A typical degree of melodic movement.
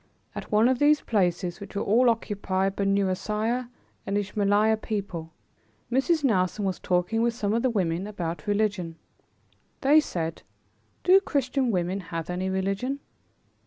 Yes: average, 4.0 semitones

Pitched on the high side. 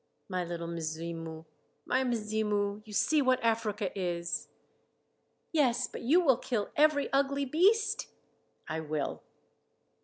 Yes: high, 215 Hz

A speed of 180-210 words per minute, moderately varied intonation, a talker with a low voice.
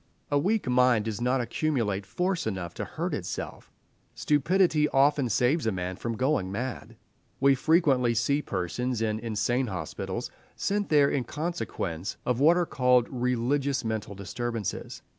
No: average, 145 wpm; average, 4.6 semitones; low, 125 Hz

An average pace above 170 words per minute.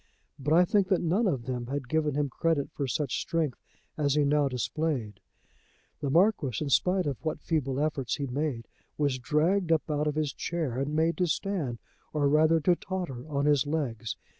Yes: average, 190 wpm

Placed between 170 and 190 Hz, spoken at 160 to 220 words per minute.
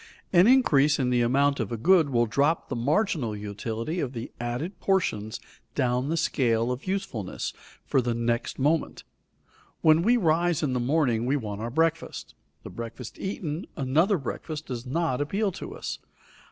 No: medium, 140 Hz; average, 165 wpm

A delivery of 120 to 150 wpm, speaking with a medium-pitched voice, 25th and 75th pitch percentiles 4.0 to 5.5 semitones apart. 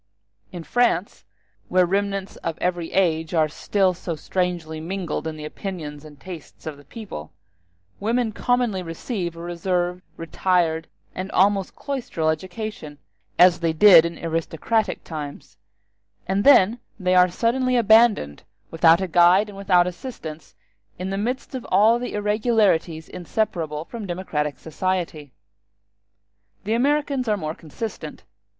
Yes: slow, 135 wpm; medium, 180 Hz; average, 4.4 semitones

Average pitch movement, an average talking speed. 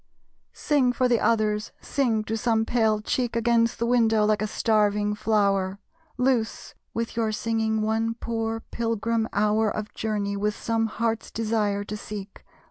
No: narrow, 1.5 semitones; average, 150 wpm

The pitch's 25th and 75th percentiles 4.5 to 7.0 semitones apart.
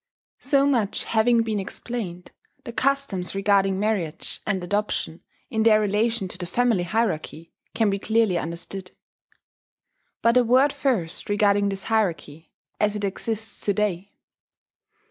No: average, 3.3 semitones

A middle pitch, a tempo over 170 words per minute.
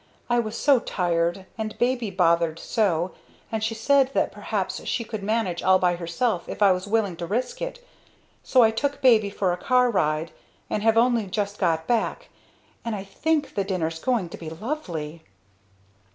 No: high, 205 Hz; average, 180 wpm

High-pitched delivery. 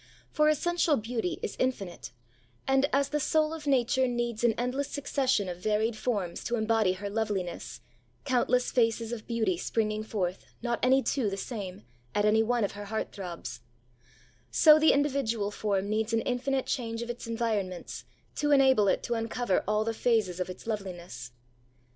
Yes: high, 225 Hz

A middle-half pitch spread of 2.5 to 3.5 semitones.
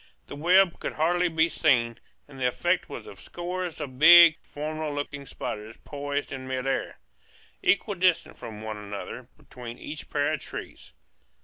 No: average, 4.8 semitones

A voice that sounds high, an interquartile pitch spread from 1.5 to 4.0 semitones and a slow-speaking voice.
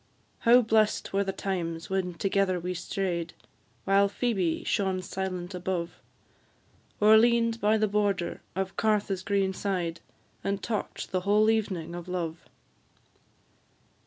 Yes: high, 195 Hz; narrow, 2.6 semitones; slow, 130 wpm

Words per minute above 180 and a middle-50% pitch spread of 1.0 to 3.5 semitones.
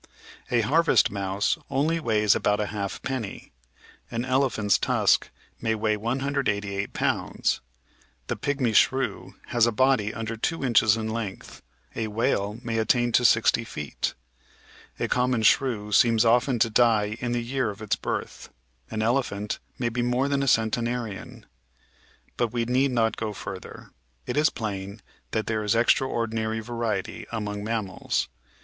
No: average, 145 wpm; average, 2.7 semitones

